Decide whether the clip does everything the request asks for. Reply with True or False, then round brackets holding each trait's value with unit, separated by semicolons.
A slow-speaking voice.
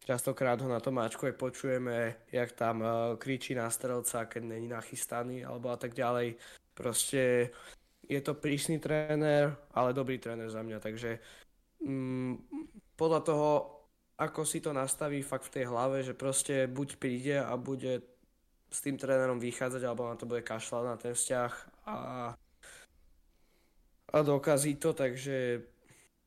False (145 wpm)